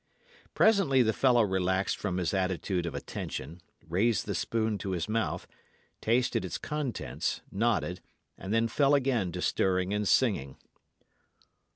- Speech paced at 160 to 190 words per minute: No, average, 140 wpm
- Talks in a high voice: No, low, 105 Hz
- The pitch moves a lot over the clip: No, average, 4.5 semitones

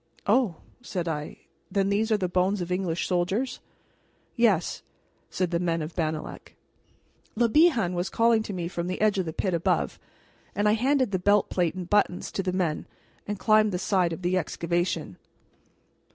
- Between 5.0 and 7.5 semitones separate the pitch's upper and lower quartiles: No, average, 3.3 semitones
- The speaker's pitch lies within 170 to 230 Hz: Yes, medium, 185 Hz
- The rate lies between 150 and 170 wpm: No, average, 180 wpm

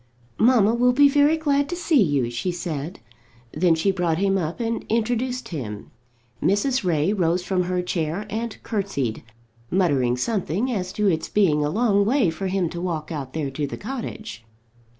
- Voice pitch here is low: No, high, 190 Hz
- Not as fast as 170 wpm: No, average, 175 wpm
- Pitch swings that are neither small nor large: No, wide, 6.2 semitones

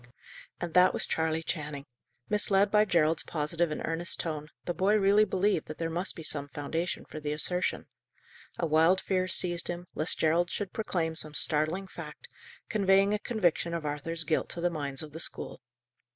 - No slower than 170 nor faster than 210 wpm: Yes, average, 180 wpm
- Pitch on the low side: No, medium, 170 Hz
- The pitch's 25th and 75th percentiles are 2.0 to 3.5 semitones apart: Yes, average, 3.2 semitones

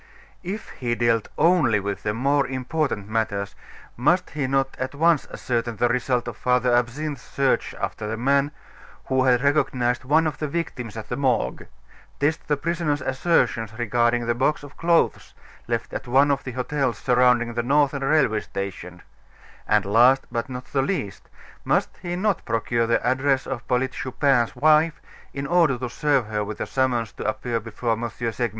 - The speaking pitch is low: Yes, low, 125 Hz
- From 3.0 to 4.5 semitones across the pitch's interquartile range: Yes, average, 3.4 semitones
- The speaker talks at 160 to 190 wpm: Yes, average, 175 wpm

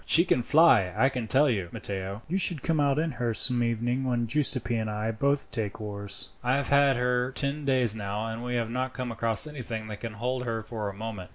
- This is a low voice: Yes, low, 120 Hz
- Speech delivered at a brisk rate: Yes, fast, 240 wpm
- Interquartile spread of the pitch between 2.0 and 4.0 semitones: Yes, average, 3.4 semitones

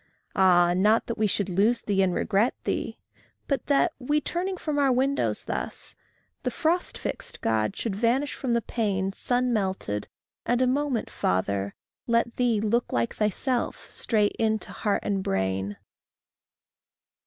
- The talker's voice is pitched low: No, high, 220 Hz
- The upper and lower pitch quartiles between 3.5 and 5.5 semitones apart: Yes, average, 4.9 semitones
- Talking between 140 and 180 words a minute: Yes, average, 150 wpm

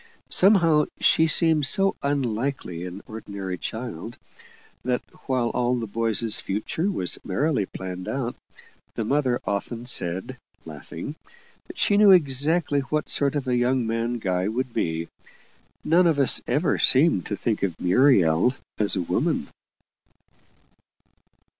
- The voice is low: Yes, low, 125 Hz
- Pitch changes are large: Yes, wide, 6.2 semitones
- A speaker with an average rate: No, slow, 130 wpm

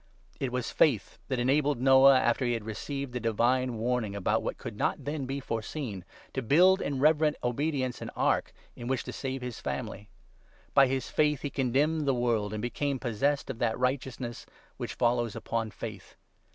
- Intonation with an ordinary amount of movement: Yes, average, 3.0 semitones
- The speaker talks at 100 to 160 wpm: No, average, 180 wpm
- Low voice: Yes, low, 125 Hz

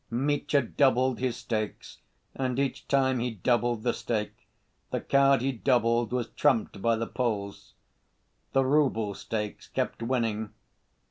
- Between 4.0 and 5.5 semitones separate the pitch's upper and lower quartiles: No, average, 2.8 semitones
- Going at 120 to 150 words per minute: Yes, slow, 135 wpm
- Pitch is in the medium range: No, low, 120 Hz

